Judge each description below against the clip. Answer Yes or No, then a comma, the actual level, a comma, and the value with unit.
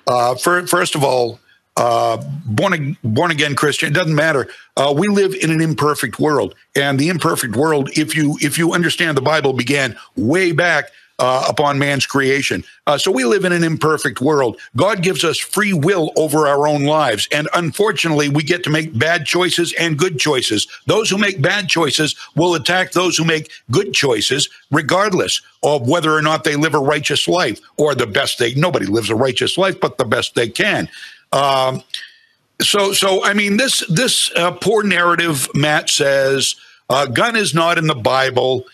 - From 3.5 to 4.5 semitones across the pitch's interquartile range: Yes, average, 3.9 semitones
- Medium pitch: Yes, medium, 155 Hz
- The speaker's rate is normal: Yes, average, 190 wpm